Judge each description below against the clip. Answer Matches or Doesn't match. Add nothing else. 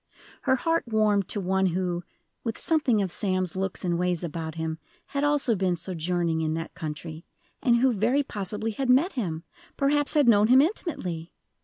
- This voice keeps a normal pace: Matches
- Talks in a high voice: Matches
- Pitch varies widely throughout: Matches